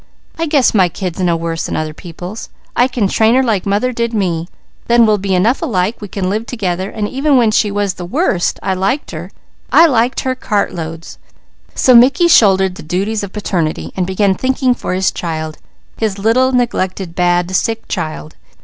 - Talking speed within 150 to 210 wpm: Yes, average, 190 wpm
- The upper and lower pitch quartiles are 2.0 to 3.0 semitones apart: No, average, 4.8 semitones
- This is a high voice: Yes, high, 200 Hz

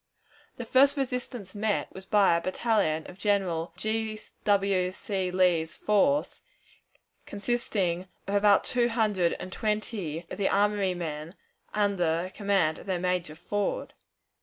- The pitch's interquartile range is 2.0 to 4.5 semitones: Yes, average, 3.0 semitones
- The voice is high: Yes, high, 200 Hz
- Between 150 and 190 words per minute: No, slow, 135 wpm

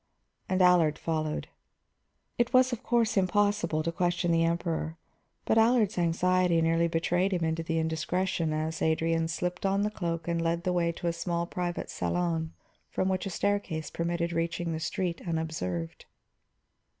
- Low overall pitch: No, medium, 170 Hz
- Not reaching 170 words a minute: Yes, average, 160 wpm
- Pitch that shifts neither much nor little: No, narrow, 1.9 semitones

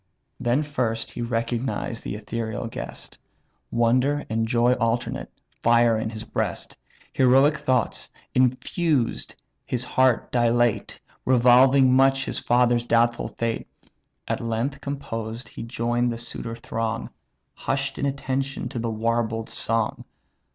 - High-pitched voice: No, low, 120 Hz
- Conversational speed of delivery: No, slow, 120 wpm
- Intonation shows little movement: Yes, narrow, 2.2 semitones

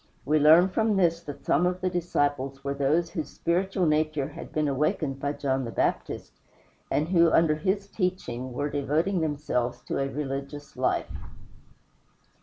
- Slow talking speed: No, average, 160 wpm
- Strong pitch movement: No, average, 3.8 semitones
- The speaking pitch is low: No, medium, 150 Hz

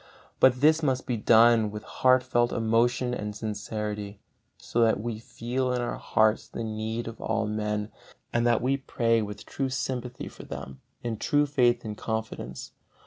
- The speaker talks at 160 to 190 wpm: Yes, average, 170 wpm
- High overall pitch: No, low, 115 Hz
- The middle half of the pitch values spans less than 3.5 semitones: Yes, narrow, 2.6 semitones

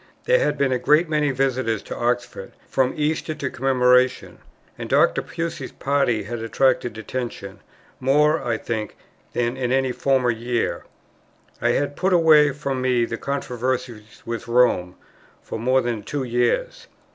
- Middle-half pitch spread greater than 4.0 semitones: No, average, 2.9 semitones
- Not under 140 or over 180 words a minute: Yes, average, 150 wpm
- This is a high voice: No, low, 130 Hz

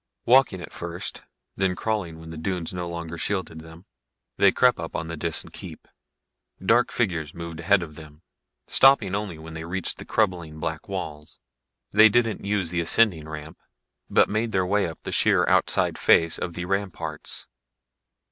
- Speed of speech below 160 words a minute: No, average, 170 wpm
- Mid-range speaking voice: No, very low, 90 Hz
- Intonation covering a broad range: No, average, 3.7 semitones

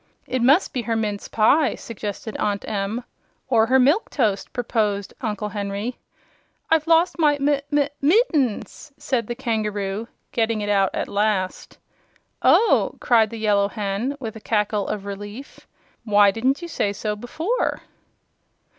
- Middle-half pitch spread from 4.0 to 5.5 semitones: Yes, average, 4.5 semitones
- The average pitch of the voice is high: Yes, high, 225 Hz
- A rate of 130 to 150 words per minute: Yes, average, 145 wpm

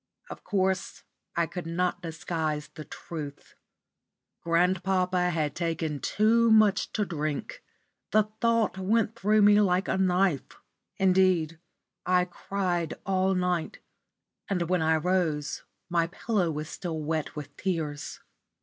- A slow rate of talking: Yes, slow, 125 wpm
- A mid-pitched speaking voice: Yes, medium, 180 Hz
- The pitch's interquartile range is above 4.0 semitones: No, average, 3.1 semitones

